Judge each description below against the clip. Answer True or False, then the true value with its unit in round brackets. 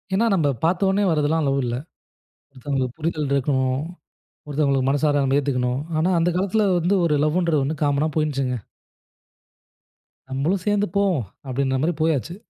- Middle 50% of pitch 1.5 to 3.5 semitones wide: False (3.9 semitones)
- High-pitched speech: False (150 Hz)